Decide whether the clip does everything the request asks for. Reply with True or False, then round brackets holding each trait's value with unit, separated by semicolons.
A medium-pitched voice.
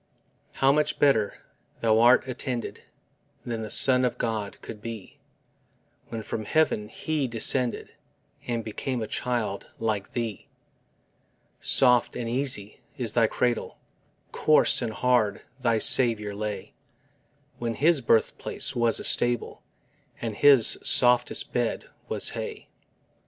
False (120 Hz)